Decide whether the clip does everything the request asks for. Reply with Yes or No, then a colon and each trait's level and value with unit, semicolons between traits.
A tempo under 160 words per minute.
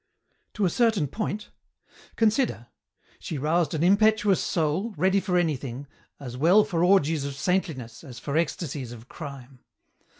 Yes: average, 140 wpm